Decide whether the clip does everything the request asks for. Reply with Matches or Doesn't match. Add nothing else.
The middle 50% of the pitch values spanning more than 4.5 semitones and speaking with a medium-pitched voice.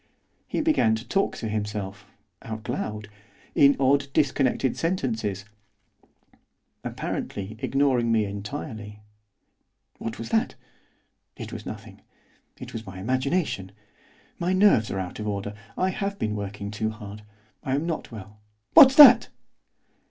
Doesn't match